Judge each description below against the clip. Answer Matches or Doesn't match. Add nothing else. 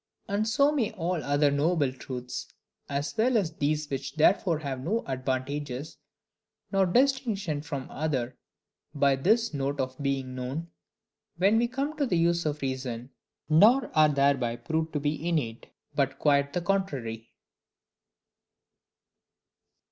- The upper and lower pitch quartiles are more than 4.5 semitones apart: Matches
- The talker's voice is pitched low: Doesn't match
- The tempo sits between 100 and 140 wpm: Matches